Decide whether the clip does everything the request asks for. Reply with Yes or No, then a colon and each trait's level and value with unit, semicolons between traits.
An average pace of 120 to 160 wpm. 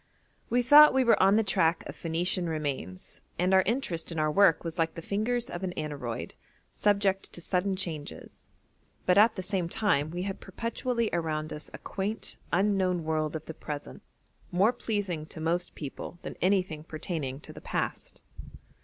No: average, 175 wpm